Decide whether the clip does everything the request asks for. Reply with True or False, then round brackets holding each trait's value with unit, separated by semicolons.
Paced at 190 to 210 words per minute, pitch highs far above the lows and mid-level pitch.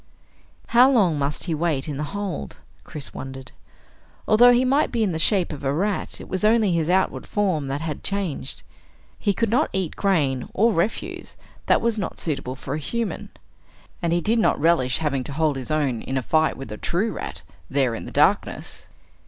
True (200 wpm; 6.6 semitones; 165 Hz)